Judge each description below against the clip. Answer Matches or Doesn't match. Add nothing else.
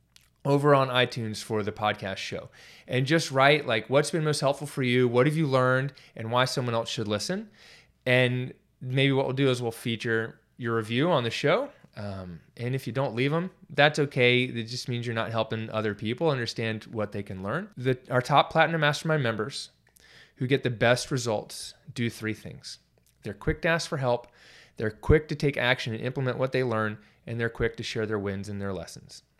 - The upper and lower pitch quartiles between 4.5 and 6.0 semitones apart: Doesn't match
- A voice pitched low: Matches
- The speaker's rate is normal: Doesn't match